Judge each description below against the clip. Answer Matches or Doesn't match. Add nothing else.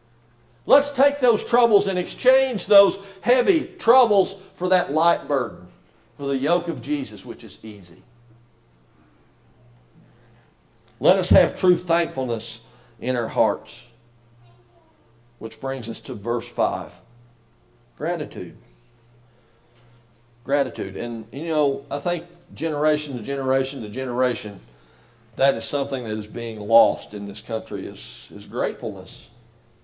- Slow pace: Matches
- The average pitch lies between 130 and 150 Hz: Doesn't match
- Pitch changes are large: Matches